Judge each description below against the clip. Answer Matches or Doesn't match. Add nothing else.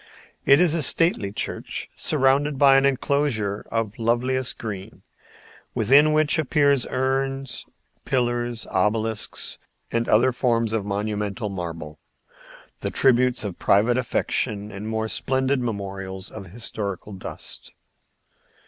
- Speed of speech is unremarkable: Doesn't match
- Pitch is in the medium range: Doesn't match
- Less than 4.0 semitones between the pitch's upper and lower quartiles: Doesn't match